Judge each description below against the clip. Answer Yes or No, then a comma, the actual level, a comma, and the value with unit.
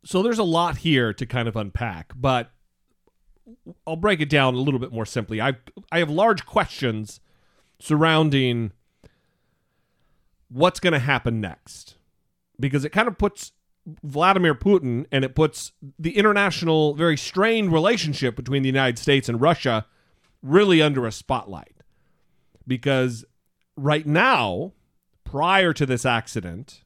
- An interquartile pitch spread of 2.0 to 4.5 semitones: No, average, 5.3 semitones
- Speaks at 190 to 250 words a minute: No, average, 140 wpm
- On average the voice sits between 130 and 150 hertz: Yes, medium, 140 Hz